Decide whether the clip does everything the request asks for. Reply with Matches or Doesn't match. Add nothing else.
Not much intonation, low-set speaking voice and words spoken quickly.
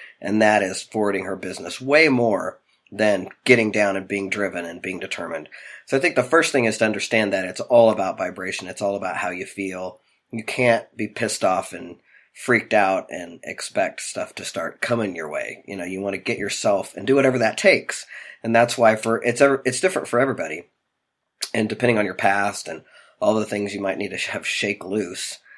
Doesn't match